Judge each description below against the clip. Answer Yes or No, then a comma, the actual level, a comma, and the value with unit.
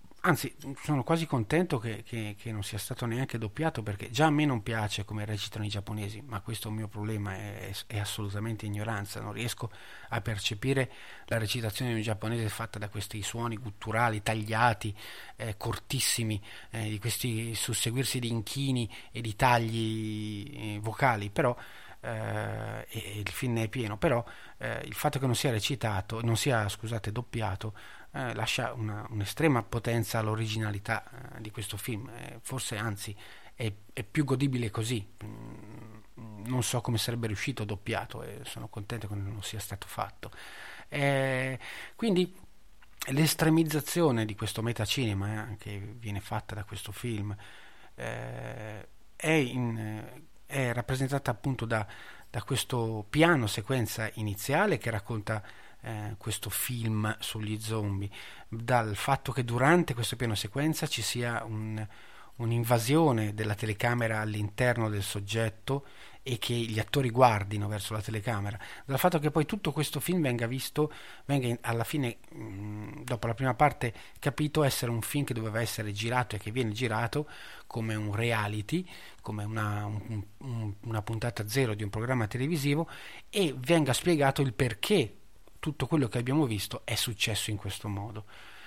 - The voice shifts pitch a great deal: No, average, 3.2 semitones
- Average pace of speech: Yes, average, 155 wpm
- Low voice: Yes, low, 115 Hz